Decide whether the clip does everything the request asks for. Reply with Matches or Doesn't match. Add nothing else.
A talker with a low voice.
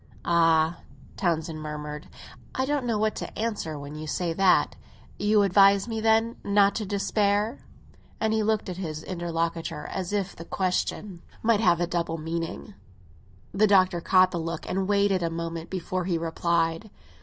Doesn't match